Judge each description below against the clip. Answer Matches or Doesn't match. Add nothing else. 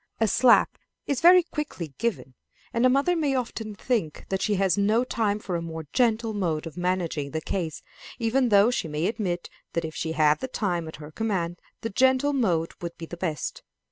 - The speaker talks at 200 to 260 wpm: Matches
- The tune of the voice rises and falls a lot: Matches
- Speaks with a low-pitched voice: Doesn't match